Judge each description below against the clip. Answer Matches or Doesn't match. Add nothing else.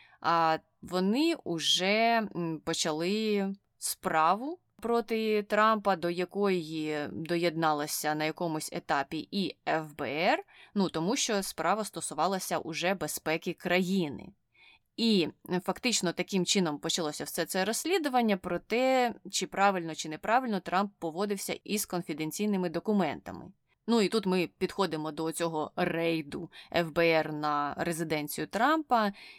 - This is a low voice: Doesn't match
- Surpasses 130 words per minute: Doesn't match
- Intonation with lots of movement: Doesn't match